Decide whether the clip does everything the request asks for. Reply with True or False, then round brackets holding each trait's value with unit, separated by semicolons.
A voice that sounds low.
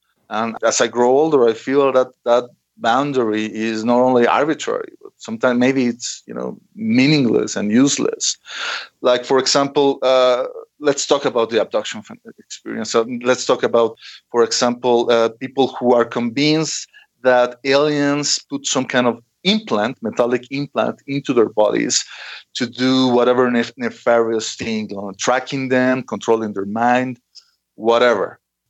True (125 Hz)